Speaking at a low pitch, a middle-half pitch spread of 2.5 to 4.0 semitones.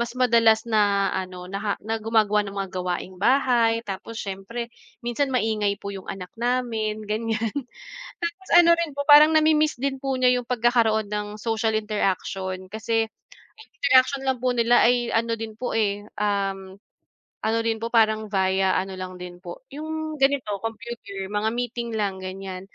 No: high, 220 Hz; average, 3.7 semitones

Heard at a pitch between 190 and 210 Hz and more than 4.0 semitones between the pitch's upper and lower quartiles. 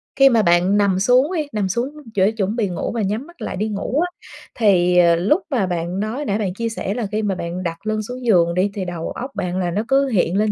Yes: high, 205 Hz; average, 4.6 semitones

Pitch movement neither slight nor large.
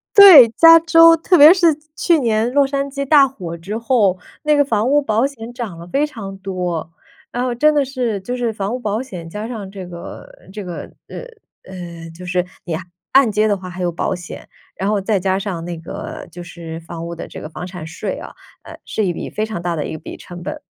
No: wide, 6.7 semitones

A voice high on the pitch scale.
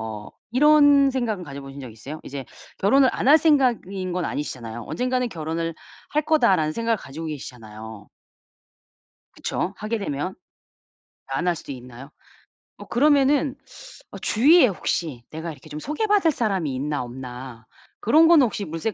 No: medium, 175 Hz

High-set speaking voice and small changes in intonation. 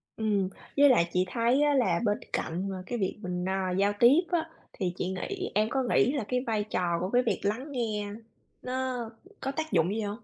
No: high, 215 Hz; average, 5.1 semitones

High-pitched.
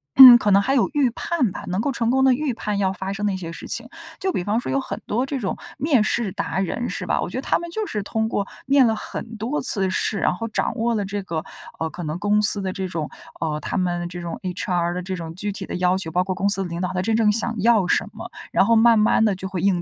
Yes: high, 200 Hz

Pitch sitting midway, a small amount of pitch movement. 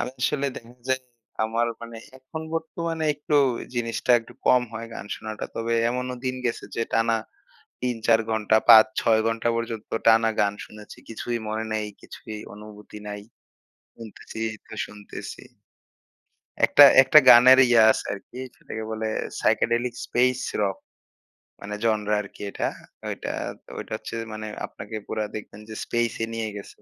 No: low, 115 Hz; narrow, 2.0 semitones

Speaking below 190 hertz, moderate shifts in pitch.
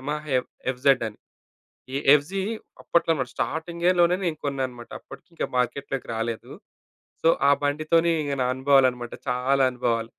Yes: medium, 140 Hz; average, 3.9 semitones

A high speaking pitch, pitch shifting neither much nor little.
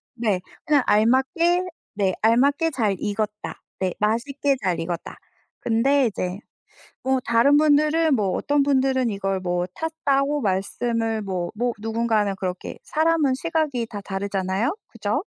No: high, 230 Hz; wide, 5.9 semitones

